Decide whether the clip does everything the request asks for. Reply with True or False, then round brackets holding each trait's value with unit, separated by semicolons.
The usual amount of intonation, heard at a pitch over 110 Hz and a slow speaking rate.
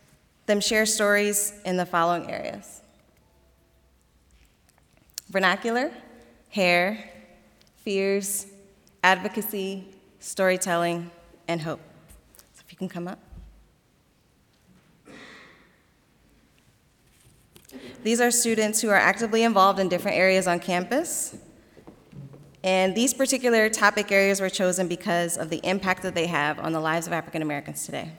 True (3.3 semitones; 185 Hz; 115 wpm)